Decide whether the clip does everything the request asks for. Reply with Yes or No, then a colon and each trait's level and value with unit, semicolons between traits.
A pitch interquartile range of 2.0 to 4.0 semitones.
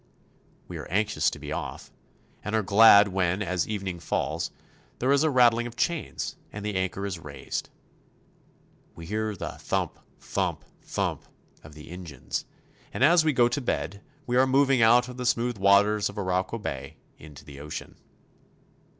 No: average, 4.8 semitones